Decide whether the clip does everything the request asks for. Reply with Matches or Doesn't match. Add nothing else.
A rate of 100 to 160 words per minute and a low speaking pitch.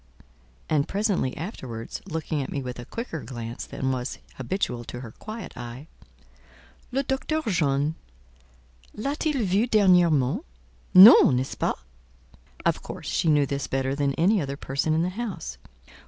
Doesn't match